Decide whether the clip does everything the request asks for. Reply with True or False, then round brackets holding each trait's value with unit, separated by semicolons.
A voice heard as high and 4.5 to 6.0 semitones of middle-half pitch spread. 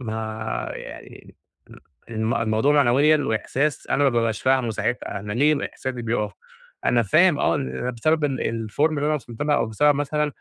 False (125 Hz; 4.8 semitones)